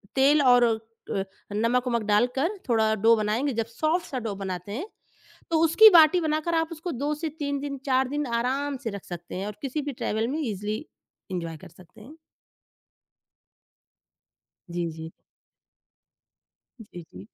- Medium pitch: No, high, 245 Hz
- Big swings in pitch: Yes, wide, 5.9 semitones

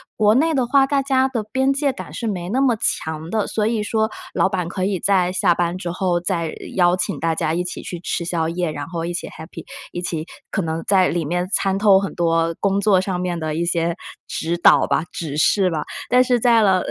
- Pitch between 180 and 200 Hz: Yes, medium, 185 Hz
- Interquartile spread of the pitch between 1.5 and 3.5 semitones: No, average, 4.1 semitones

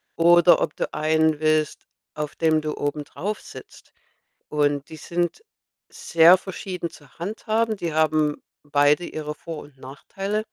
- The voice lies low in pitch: No, medium, 155 Hz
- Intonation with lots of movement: No, narrow, 2.5 semitones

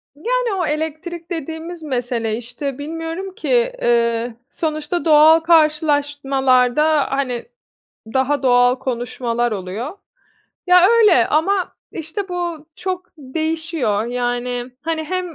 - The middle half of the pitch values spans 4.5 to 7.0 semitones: Yes, average, 5.2 semitones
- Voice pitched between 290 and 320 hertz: Yes, very high, 300 Hz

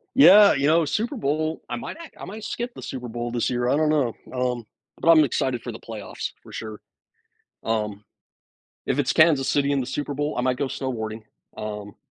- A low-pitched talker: Yes, low, 130 Hz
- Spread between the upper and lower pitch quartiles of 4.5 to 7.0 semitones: Yes, average, 4.9 semitones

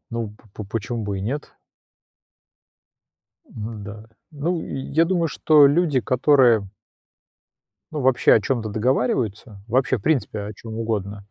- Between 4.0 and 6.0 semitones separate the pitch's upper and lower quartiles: Yes, average, 4.8 semitones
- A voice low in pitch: Yes, low, 115 Hz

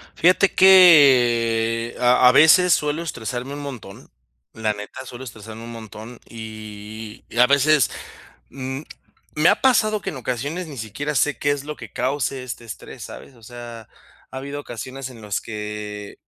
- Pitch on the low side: Yes, low, 125 Hz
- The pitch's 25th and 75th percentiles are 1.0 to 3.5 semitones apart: No, average, 4.3 semitones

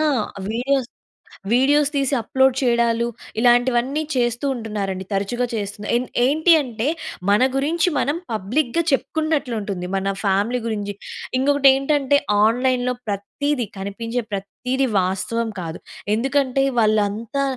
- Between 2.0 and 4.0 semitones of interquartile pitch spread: No, average, 4.4 semitones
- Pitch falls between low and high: No, high, 245 Hz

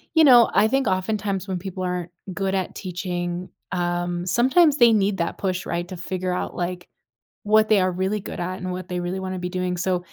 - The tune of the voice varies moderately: No, narrow, 2.0 semitones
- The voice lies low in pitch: No, medium, 185 Hz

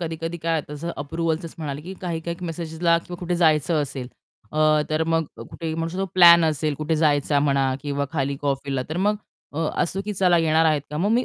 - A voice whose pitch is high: No, medium, 160 Hz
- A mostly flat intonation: Yes, narrow, 2.3 semitones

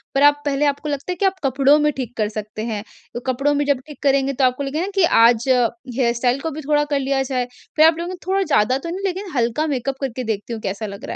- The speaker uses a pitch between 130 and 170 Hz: No, very high, 275 Hz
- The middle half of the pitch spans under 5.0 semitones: Yes, average, 3.6 semitones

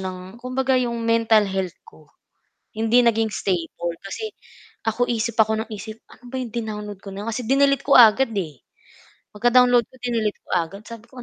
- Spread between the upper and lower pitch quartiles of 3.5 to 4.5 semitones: No, average, 3.0 semitones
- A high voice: Yes, high, 225 Hz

